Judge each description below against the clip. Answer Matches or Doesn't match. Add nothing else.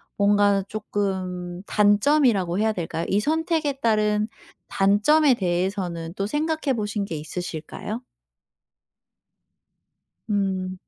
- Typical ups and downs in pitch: Matches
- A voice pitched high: Matches